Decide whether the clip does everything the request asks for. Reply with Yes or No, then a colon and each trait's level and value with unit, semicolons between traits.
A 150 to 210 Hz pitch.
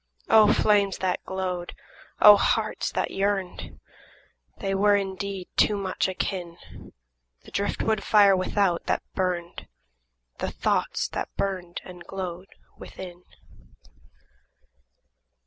Yes: high, 190 Hz